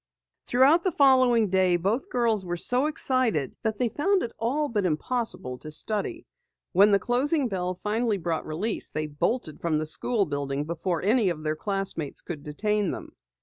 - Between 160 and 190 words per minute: Yes, average, 175 wpm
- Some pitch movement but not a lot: No, wide, 6.9 semitones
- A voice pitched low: No, high, 205 Hz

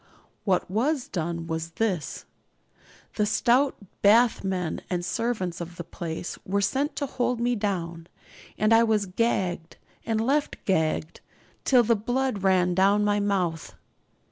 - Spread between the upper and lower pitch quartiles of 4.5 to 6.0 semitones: Yes, average, 4.8 semitones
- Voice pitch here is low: No, high, 200 Hz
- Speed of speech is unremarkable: Yes, average, 145 wpm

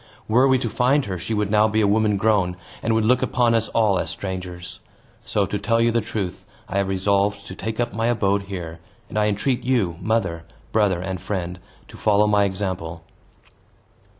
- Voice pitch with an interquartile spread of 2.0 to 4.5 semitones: Yes, average, 3.0 semitones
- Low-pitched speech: Yes, low, 105 Hz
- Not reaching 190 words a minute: No, average, 200 wpm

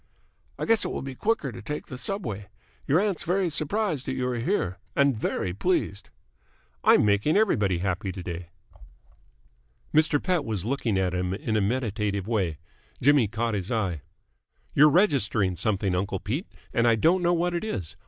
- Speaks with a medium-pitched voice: No, low, 115 Hz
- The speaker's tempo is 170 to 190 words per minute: Yes, average, 175 wpm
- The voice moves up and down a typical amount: No, wide, 8.0 semitones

